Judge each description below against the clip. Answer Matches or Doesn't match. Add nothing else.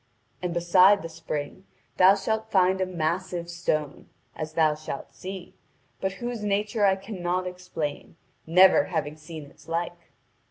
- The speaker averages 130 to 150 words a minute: Matches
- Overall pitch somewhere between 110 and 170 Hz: Doesn't match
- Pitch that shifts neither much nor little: Matches